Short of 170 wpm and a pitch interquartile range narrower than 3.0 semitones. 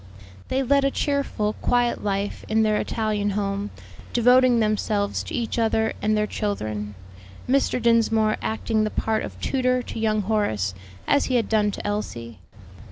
Yes: average, 160 wpm; narrow, 2.6 semitones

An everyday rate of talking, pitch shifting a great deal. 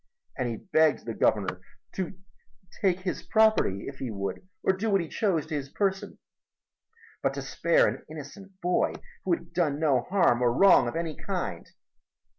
Yes: average, 180 wpm; wide, 7.1 semitones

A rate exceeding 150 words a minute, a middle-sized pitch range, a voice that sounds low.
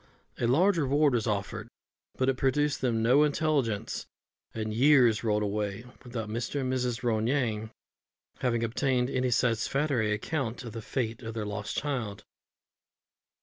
No: average, 145 wpm; average, 3.5 semitones; low, 120 Hz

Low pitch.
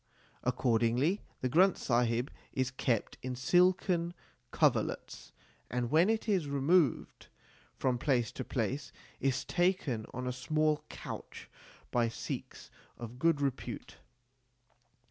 Yes: low, 130 Hz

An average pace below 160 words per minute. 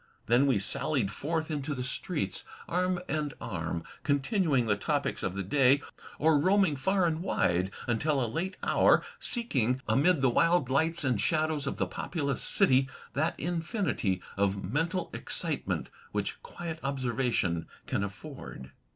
Yes: average, 150 wpm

